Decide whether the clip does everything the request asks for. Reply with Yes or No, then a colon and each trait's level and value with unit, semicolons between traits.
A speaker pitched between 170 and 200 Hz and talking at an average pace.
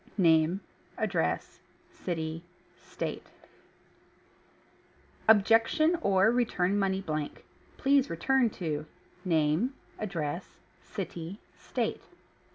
No: high, 190 Hz; slow, 75 wpm